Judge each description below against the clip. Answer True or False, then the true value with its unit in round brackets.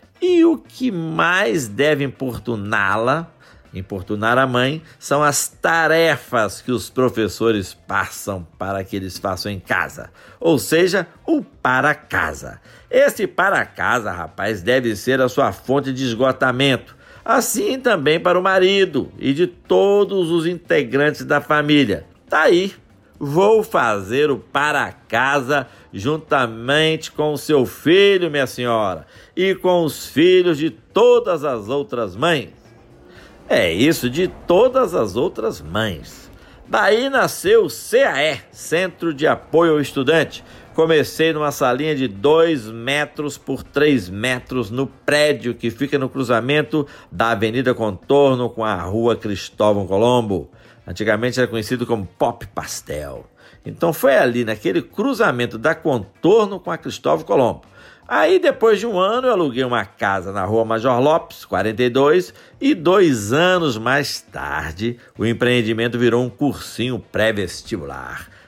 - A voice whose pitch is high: False (130 Hz)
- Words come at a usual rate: True (135 wpm)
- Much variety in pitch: True (6.0 semitones)